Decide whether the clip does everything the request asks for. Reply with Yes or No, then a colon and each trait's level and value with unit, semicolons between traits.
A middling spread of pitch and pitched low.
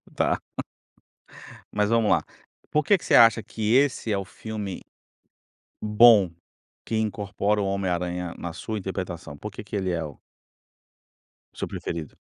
Yes: average, 3.4 semitones; low, 100 Hz